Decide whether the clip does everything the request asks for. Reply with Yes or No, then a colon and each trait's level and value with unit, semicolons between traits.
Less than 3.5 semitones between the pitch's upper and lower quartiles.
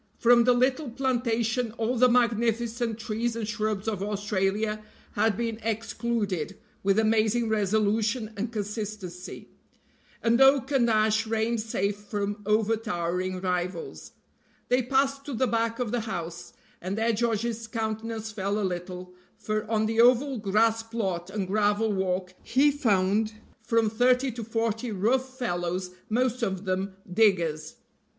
Yes: average, 2.7 semitones